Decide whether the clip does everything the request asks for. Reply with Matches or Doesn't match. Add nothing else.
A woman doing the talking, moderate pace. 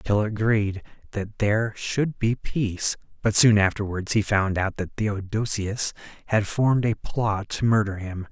Doesn't match